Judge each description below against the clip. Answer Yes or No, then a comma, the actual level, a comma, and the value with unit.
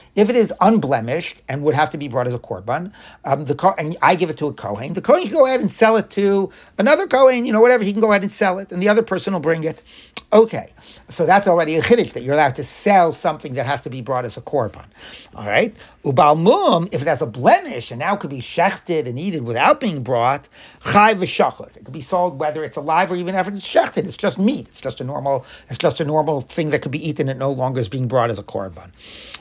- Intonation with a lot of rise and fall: Yes, wide, 6.4 semitones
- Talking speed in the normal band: No, fast, 265 wpm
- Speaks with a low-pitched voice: No, medium, 160 Hz